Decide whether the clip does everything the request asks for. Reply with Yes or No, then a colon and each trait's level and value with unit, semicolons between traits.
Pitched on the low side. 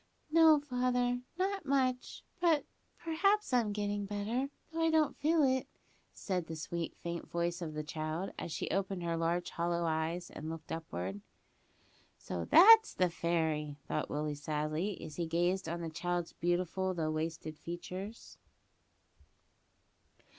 No: medium, 175 Hz